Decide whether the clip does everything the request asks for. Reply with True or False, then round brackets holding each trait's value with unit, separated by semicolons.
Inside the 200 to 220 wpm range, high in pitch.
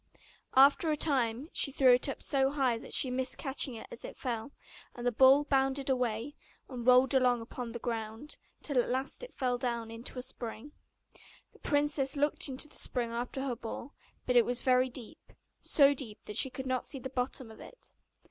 True (205 wpm; 255 Hz)